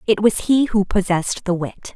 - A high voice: Yes, high, 200 Hz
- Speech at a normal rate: No, fast, 215 wpm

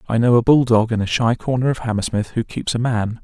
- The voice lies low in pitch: Yes, low, 115 Hz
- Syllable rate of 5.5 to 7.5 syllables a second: Yes, 5.9 syllables/s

